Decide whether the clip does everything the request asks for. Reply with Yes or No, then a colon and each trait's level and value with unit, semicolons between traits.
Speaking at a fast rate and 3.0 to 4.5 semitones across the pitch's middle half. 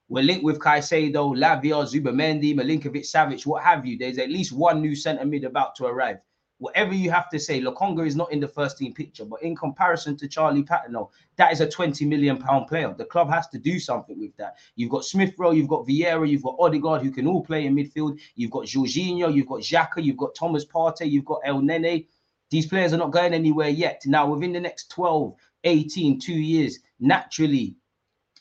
No: fast, 210 wpm; narrow, 2.6 semitones